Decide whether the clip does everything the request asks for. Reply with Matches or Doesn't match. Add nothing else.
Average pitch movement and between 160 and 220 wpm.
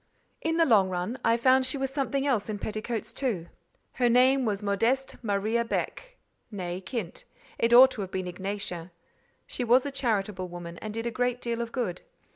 Matches